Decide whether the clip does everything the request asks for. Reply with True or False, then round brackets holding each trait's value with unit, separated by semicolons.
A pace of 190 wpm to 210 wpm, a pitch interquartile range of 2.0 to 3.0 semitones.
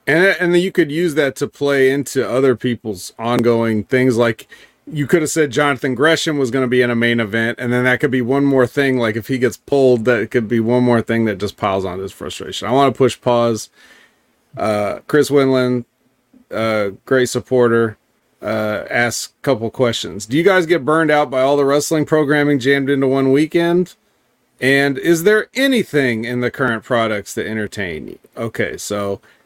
False (200 wpm; 3.8 semitones)